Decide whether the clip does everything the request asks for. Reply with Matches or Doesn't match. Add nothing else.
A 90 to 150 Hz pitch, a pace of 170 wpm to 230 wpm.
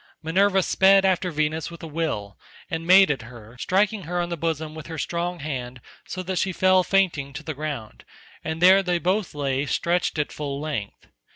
Doesn't match